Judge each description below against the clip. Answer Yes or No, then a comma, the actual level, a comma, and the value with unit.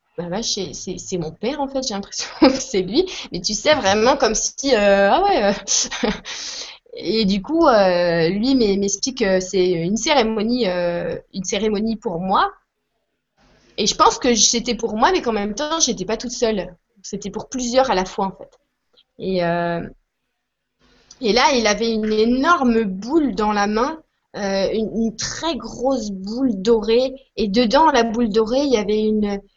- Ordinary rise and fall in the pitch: Yes, average, 4.3 semitones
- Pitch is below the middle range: No, high, 220 Hz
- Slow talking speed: No, average, 175 wpm